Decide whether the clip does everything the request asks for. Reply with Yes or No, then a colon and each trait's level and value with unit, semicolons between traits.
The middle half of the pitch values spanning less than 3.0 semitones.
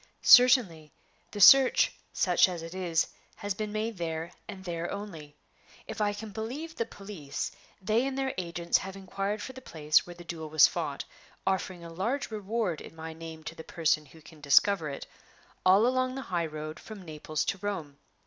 No: average, 4.9 semitones